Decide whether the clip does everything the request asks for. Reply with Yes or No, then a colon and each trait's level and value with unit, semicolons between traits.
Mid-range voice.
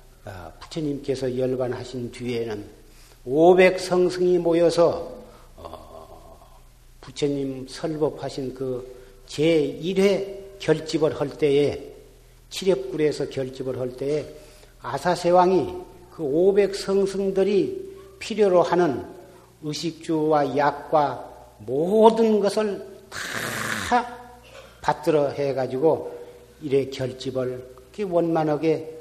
Yes: medium, 155 Hz